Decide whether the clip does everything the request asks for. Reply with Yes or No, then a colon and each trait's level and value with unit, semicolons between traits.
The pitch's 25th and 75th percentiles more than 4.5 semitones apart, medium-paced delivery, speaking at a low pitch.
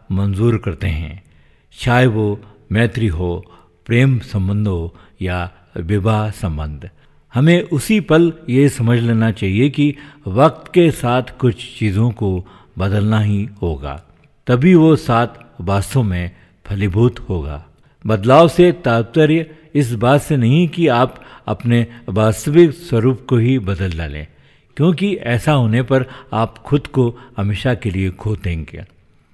Yes: wide, 5.5 semitones; average, 135 wpm; low, 115 Hz